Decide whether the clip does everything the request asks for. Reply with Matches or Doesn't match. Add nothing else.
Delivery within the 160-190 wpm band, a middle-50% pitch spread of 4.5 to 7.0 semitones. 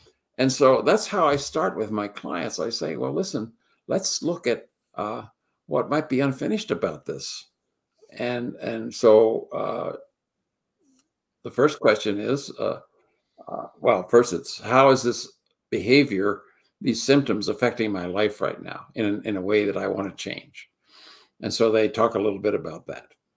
Matches